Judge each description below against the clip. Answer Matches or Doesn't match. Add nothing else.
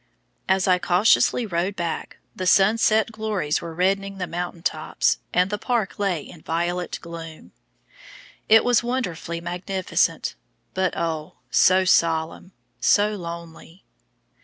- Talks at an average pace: Doesn't match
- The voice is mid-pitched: Matches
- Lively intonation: Doesn't match